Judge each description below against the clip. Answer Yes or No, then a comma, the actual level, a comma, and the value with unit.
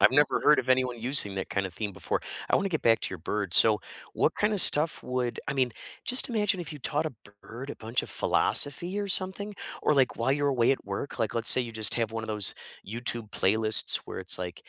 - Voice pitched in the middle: No, low, 125 Hz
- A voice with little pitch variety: No, average, 5.3 semitones